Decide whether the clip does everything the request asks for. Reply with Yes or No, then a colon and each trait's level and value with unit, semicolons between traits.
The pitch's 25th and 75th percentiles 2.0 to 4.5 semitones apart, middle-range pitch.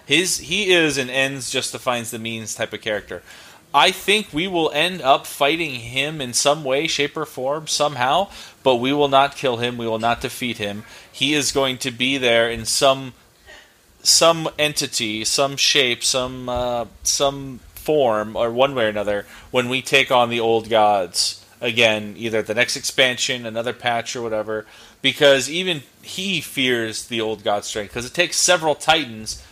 No: average, 3.9 semitones; low, 125 Hz